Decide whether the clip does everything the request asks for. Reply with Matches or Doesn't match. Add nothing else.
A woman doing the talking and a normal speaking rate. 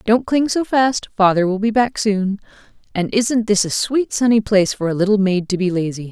Doesn't match